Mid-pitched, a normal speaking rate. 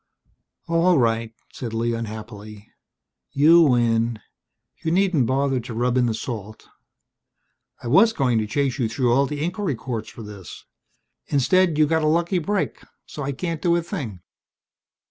No: low, 130 Hz; average, 160 wpm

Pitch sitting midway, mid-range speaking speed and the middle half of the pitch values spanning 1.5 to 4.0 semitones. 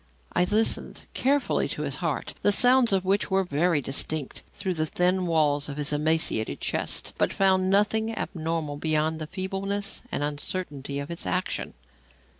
No: medium, 170 Hz; average, 160 wpm; average, 4.6 semitones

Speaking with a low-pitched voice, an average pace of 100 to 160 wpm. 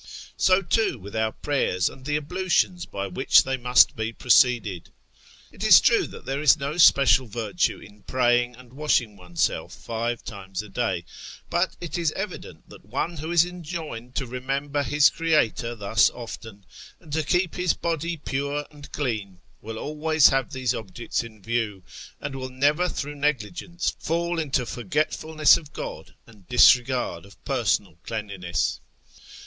Yes: low, 130 Hz; average, 155 wpm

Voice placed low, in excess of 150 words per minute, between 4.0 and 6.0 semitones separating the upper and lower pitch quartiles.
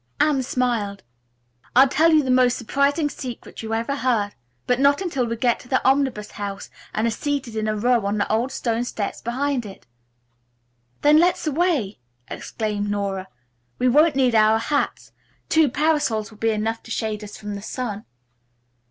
No: high, 240 Hz; average, 175 wpm; average, 4.5 semitones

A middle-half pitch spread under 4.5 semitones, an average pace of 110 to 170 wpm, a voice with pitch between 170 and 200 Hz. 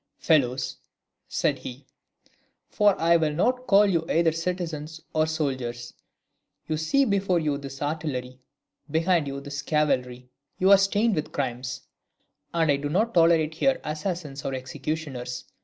No: average, 3.9 semitones; average, 140 wpm; medium, 155 Hz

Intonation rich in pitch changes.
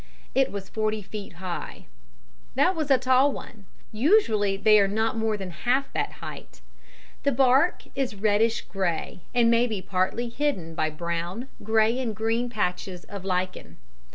No: average, 4.3 semitones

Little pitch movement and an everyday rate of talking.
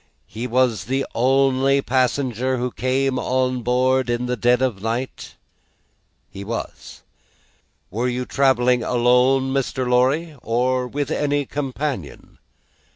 No: narrow, 1.4 semitones; slow, 125 wpm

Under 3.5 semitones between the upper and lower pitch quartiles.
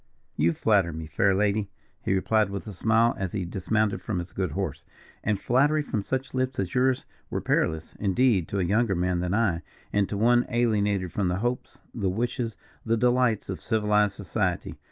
No: average, 3.8 semitones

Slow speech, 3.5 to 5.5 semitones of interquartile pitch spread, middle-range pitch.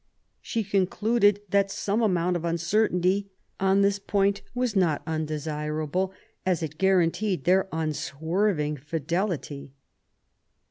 Yes: slow, 105 wpm; average, 4.0 semitones; medium, 180 Hz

